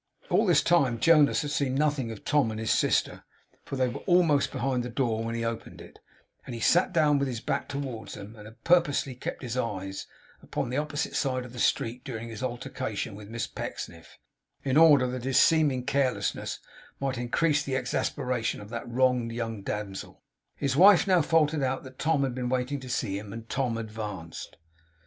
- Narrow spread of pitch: No, average, 3.8 semitones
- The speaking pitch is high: No, low, 125 Hz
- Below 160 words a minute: No, average, 200 wpm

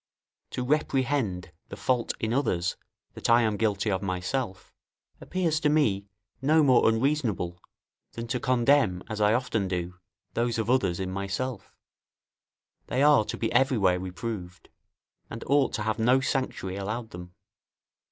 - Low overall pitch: Yes, low, 115 Hz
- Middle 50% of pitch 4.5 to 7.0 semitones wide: Yes, average, 5.3 semitones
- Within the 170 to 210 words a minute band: No, average, 145 wpm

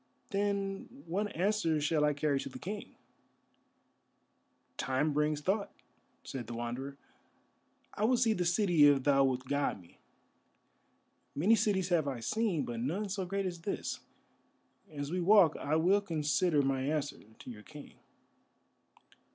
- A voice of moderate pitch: Yes, medium, 155 Hz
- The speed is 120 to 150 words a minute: Yes, average, 145 wpm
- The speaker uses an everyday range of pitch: No, wide, 5.8 semitones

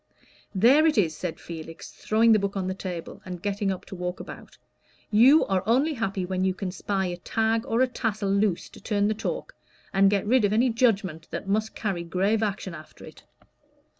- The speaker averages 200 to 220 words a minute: Yes, fast, 205 wpm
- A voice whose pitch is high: Yes, high, 200 Hz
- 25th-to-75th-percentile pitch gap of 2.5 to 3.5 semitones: Yes, average, 3.2 semitones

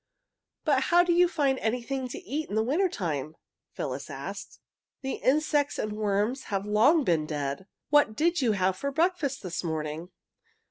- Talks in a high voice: Yes, very high, 250 Hz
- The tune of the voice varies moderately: No, wide, 7.6 semitones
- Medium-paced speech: Yes, average, 170 wpm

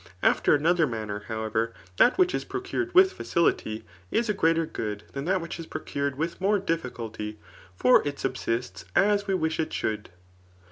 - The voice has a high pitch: No, medium, 155 Hz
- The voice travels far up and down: Yes, wide, 9.0 semitones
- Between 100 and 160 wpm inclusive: No, average, 170 wpm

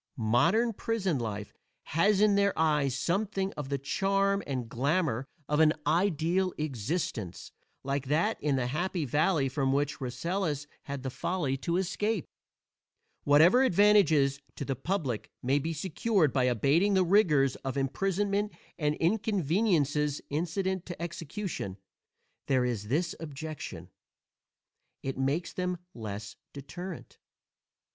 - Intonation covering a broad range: Yes, wide, 5.8 semitones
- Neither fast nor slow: No, slow, 125 wpm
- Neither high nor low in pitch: Yes, medium, 155 Hz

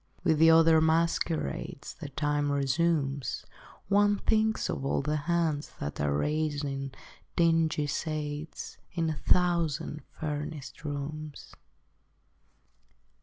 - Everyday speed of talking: No, slow, 105 wpm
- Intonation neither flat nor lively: No, narrow, 2.3 semitones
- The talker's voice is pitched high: No, medium, 155 Hz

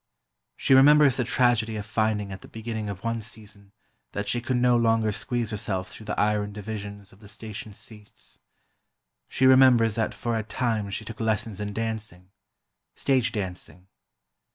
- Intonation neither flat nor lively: No, narrow, 2.2 semitones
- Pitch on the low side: Yes, low, 110 Hz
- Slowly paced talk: No, average, 160 wpm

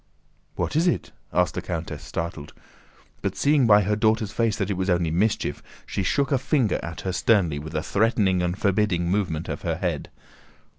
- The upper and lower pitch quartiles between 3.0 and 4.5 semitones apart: Yes, average, 4.2 semitones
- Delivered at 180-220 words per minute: Yes, average, 190 wpm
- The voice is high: No, low, 100 Hz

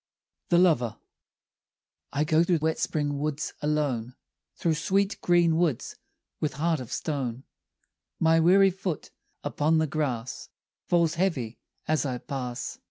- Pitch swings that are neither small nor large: Yes, average, 3.8 semitones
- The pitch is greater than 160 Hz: No, medium, 155 Hz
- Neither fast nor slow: No, slow, 130 wpm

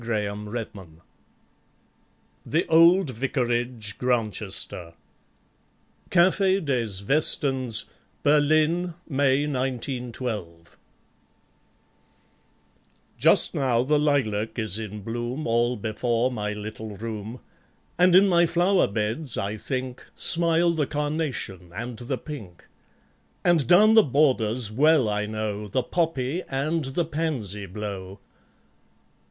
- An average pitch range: No, wide, 6.1 semitones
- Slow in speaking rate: Yes, slow, 100 wpm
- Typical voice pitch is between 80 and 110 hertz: No, low, 125 Hz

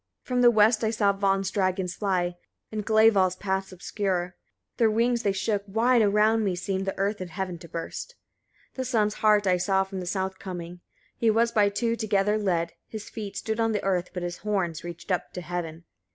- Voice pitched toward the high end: Yes, high, 195 Hz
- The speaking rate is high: Yes, fast, 210 wpm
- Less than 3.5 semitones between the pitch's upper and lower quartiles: Yes, average, 2.8 semitones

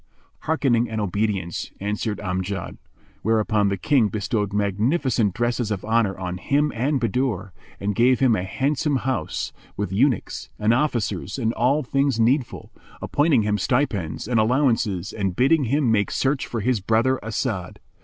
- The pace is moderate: Yes, average, 150 wpm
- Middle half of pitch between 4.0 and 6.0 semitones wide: Yes, average, 4.3 semitones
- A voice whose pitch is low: Yes, low, 115 Hz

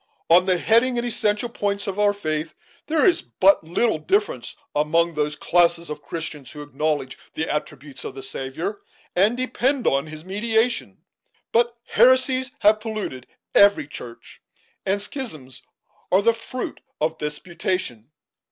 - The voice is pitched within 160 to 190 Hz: Yes, medium, 185 Hz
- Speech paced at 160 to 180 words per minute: No, average, 145 wpm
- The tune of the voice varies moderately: No, wide, 7.1 semitones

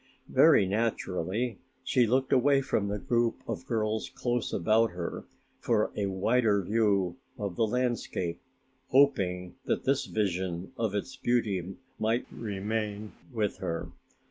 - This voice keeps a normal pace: No, slow, 130 wpm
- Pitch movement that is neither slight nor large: Yes, average, 3.8 semitones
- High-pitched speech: No, low, 110 Hz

